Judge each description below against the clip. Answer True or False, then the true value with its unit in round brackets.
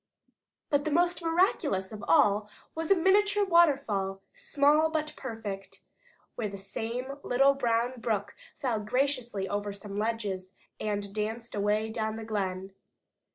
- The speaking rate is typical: False (130 wpm)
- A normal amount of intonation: False (6.1 semitones)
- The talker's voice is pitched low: False (230 Hz)